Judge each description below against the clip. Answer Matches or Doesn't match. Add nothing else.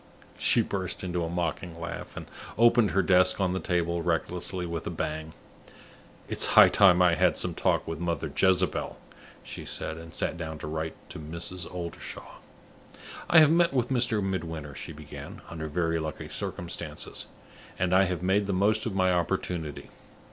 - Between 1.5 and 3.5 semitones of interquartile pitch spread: Matches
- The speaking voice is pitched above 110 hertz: Doesn't match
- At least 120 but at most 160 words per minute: Doesn't match